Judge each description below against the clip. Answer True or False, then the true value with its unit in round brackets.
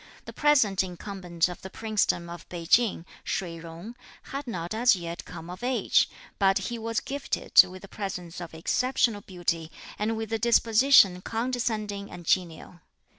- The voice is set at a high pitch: True (195 Hz)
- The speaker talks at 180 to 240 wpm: False (160 wpm)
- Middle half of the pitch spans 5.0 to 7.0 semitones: False (4.6 semitones)